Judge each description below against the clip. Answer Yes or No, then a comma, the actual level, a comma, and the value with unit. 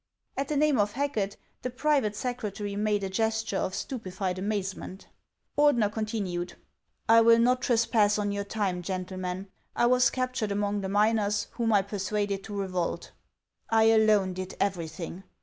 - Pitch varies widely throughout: No, average, 2.8 semitones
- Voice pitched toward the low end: No, high, 205 Hz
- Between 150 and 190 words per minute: Yes, average, 155 wpm